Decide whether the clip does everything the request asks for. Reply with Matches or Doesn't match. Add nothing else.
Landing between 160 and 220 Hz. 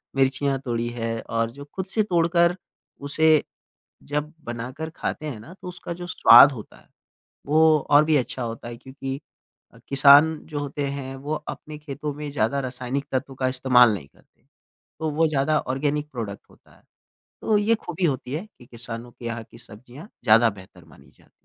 Doesn't match